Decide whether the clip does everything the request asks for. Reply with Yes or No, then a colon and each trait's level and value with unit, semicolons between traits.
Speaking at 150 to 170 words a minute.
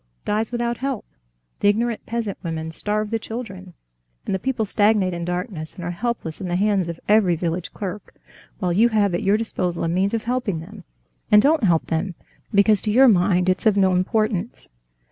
No: average, 195 wpm